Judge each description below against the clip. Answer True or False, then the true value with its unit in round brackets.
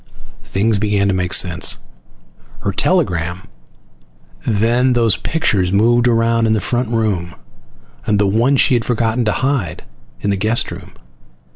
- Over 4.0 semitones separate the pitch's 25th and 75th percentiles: False (3.4 semitones)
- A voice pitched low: True (110 Hz)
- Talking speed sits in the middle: True (145 wpm)